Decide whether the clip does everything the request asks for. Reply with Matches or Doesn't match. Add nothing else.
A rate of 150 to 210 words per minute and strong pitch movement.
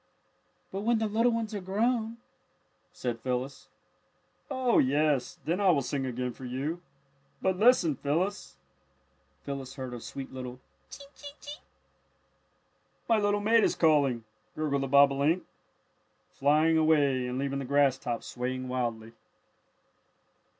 Doesn't match